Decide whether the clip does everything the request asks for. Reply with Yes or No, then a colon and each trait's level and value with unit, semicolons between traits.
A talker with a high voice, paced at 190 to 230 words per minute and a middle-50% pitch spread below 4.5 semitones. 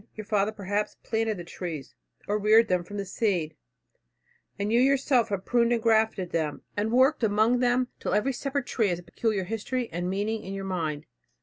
Yes: high, 210 Hz; average, 195 wpm; average, 3.7 semitones